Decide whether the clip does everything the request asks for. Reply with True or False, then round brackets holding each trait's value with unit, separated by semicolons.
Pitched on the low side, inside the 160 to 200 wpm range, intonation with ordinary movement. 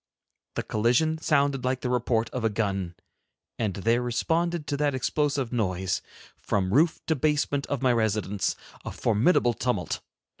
False (125 Hz; 150 wpm; 4.9 semitones)